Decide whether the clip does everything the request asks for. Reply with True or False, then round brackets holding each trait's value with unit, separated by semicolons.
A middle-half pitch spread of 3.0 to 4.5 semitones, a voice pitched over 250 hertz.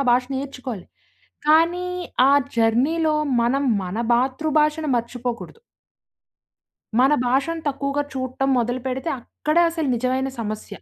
True (3.9 semitones; 265 Hz)